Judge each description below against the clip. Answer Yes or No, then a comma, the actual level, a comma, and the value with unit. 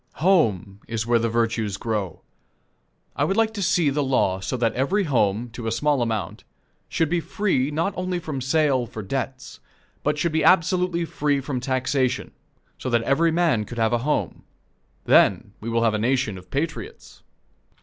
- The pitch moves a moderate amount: No, wide, 5.9 semitones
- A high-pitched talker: No, low, 130 Hz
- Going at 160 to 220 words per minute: Yes, average, 180 wpm